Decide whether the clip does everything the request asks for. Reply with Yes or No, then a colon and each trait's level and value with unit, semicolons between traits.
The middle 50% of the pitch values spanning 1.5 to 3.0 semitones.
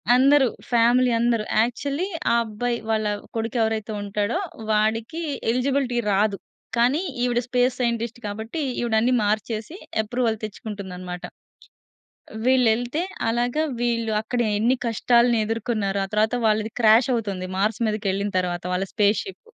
Yes: narrow, 2.6 semitones